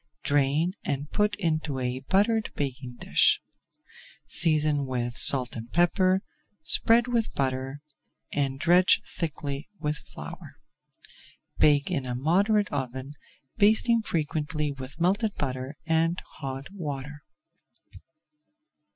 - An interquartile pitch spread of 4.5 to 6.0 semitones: Yes, average, 5.1 semitones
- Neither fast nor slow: No, slow, 110 wpm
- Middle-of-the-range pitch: Yes, medium, 150 Hz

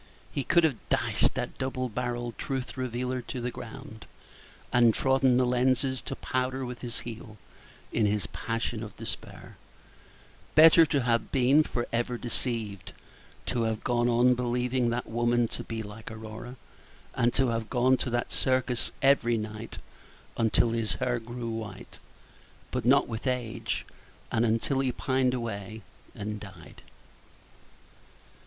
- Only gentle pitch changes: Yes, narrow, 2.2 semitones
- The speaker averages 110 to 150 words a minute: Yes, average, 145 wpm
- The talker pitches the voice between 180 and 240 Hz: No, low, 120 Hz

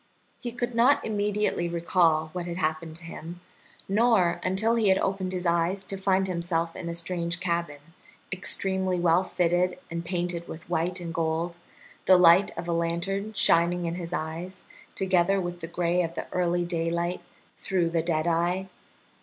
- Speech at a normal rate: Yes, average, 170 wpm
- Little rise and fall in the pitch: Yes, narrow, 1.9 semitones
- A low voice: No, medium, 175 Hz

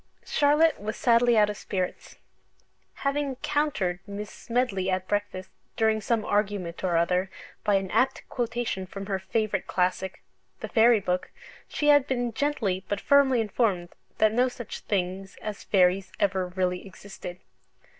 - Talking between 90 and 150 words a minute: Yes, average, 145 wpm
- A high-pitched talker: Yes, high, 205 Hz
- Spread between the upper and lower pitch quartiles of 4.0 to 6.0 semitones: Yes, average, 4.4 semitones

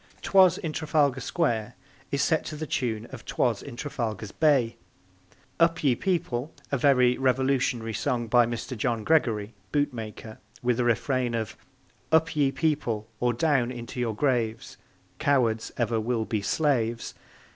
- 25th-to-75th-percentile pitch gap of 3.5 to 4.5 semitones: Yes, average, 3.9 semitones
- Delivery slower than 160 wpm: Yes, average, 150 wpm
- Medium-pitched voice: No, low, 125 Hz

